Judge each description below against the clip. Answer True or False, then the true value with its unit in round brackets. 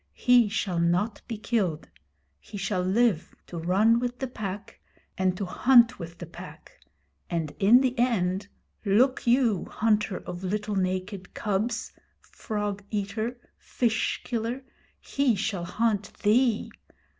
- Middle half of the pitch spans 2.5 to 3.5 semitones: False (3.9 semitones)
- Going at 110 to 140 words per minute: True (135 wpm)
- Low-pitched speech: False (210 Hz)